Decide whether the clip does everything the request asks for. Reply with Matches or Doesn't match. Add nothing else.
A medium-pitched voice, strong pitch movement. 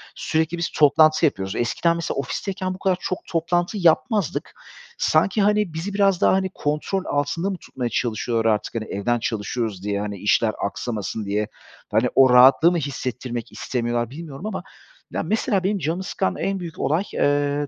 Matches